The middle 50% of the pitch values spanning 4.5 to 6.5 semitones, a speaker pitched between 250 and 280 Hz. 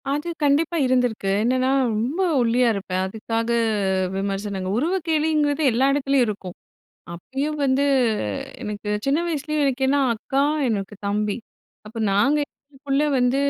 Yes: average, 5.2 semitones; very high, 255 Hz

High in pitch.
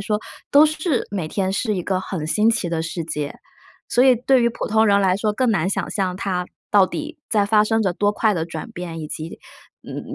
Yes: high, 200 Hz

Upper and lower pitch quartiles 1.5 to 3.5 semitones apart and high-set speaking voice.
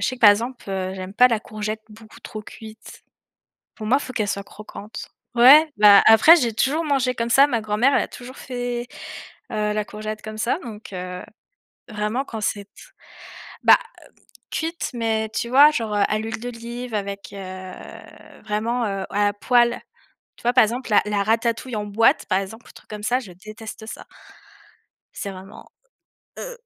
Yes: average, 2.8 semitones; high, 220 Hz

